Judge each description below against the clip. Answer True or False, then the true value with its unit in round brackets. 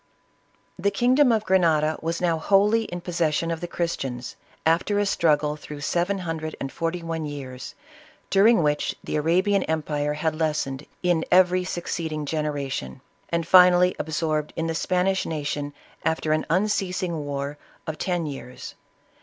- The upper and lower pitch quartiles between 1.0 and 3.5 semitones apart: True (3.2 semitones)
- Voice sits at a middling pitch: True (165 Hz)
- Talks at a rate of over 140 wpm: True (155 wpm)